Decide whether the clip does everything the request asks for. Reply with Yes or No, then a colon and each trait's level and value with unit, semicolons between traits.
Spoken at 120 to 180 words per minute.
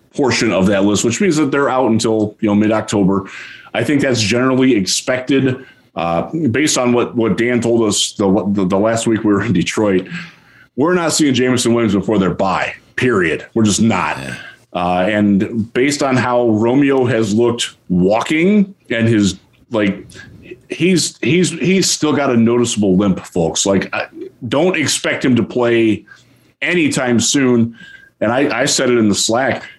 Yes: average, 175 wpm